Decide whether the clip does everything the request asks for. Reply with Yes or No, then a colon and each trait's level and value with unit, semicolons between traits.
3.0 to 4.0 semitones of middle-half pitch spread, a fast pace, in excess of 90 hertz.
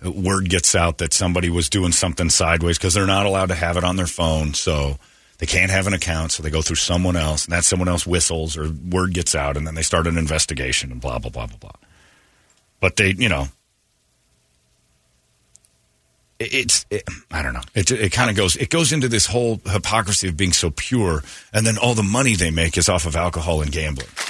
No: average, 3.4 semitones; fast, 220 wpm; very low, 85 Hz